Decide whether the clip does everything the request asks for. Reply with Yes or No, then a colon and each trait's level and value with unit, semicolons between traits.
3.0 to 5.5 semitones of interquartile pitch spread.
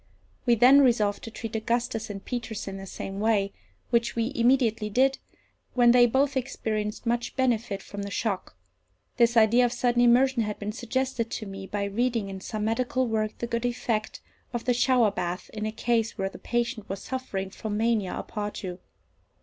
No: narrow, 2.6 semitones